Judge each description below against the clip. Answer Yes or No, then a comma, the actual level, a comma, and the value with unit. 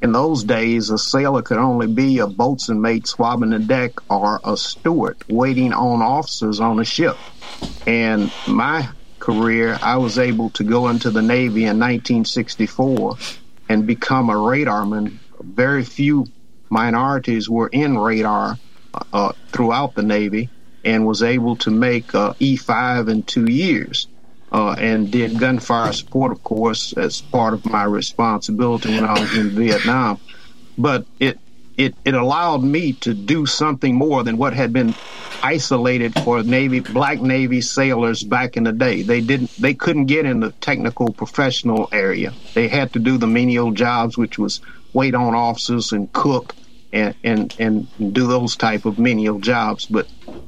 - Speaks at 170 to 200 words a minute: No, average, 160 wpm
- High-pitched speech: No, low, 120 Hz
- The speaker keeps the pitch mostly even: Yes, narrow, 2.3 semitones